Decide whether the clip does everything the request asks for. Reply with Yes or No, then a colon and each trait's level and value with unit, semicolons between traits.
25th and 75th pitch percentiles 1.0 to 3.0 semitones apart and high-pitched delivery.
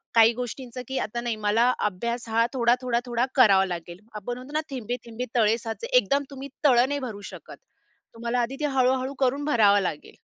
Yes: average, 2.7 semitones; high, 240 Hz